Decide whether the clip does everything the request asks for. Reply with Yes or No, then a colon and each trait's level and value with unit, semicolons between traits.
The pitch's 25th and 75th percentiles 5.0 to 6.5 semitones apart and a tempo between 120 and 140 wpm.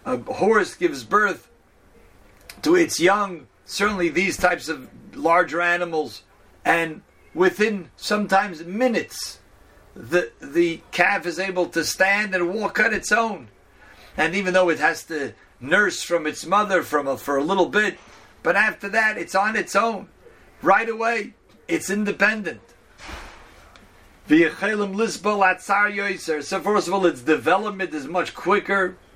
No: average, 3.7 semitones; slow, 135 wpm